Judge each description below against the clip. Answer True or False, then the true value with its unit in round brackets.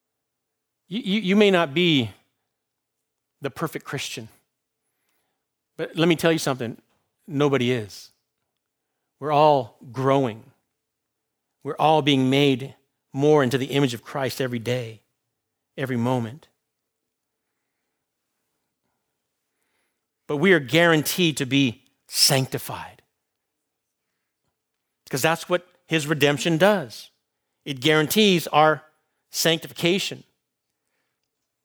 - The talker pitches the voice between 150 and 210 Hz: False (140 Hz)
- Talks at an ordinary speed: False (95 wpm)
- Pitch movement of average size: True (3.8 semitones)